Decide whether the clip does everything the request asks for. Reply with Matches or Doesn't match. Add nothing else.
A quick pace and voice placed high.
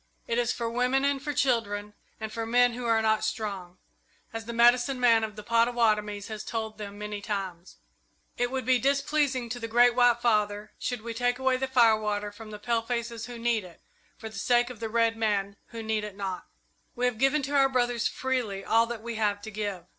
Matches